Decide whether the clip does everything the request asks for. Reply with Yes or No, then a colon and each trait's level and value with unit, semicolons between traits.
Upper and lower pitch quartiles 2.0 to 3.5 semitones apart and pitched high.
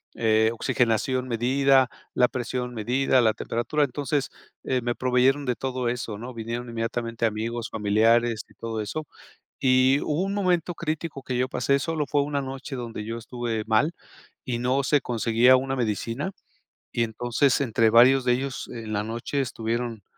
No: average, 2.8 semitones; low, 125 Hz